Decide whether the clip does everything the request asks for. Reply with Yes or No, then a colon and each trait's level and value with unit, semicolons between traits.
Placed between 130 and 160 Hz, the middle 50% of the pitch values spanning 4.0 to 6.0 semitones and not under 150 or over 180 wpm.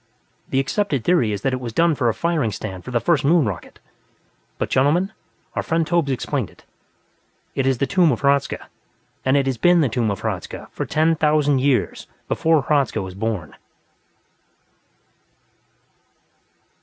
Yes: low, 135 Hz; wide, 5.4 semitones; average, 165 wpm